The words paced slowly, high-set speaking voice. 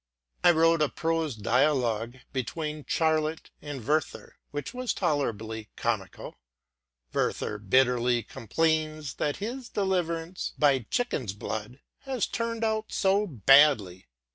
No: slow, 115 wpm; medium, 150 Hz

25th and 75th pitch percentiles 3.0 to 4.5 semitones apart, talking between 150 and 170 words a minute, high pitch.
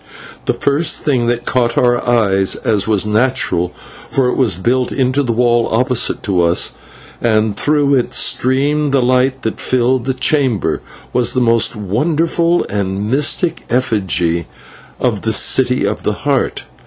No: average, 3.6 semitones; average, 155 wpm; low, 120 Hz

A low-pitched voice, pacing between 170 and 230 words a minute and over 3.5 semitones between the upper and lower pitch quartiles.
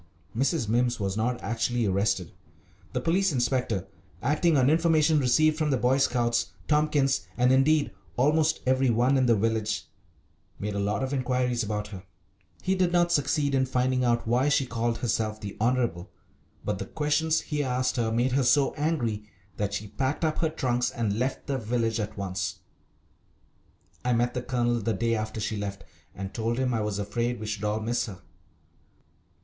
Yes: low, 120 Hz; average, 180 wpm; average, 4.0 semitones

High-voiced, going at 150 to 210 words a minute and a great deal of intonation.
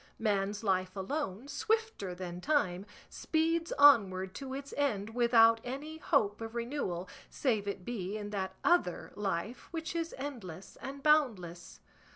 No: high, 225 Hz; average, 140 wpm; wide, 7.0 semitones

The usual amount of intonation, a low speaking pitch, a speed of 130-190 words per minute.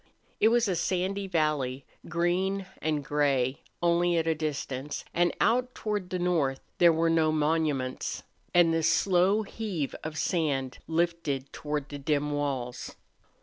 No: average, 3.4 semitones; medium, 160 Hz; average, 145 wpm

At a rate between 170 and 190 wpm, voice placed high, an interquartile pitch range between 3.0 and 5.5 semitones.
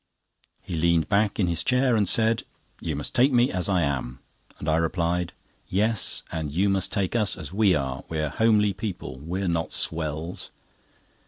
No: average, 175 wpm; very low, 90 Hz; average, 4.7 semitones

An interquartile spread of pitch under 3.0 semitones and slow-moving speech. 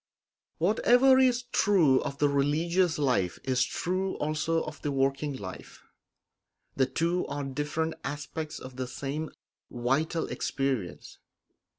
No: average, 3.6 semitones; slow, 120 wpm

